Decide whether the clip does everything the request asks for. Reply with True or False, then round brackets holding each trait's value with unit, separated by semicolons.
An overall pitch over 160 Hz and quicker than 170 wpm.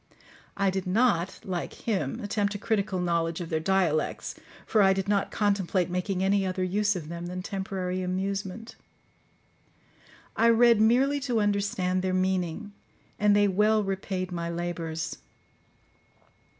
False (190 Hz; 140 wpm)